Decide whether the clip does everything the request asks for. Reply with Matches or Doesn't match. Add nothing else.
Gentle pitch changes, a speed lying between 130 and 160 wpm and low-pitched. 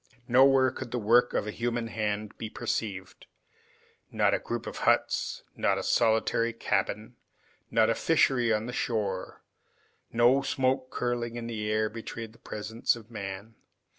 Matches